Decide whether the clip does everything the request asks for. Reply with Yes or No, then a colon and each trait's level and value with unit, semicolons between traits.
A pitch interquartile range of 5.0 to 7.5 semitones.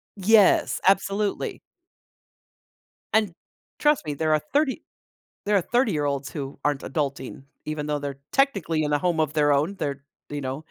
Yes: wide, 5.5 semitones